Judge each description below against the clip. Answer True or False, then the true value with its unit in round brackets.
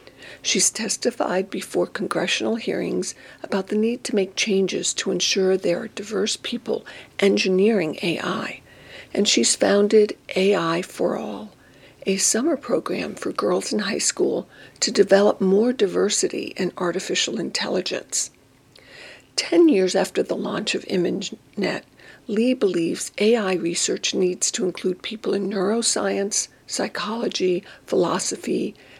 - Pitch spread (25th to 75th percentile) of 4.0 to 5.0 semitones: False (3.0 semitones)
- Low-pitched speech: False (200 Hz)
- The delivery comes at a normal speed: False (120 wpm)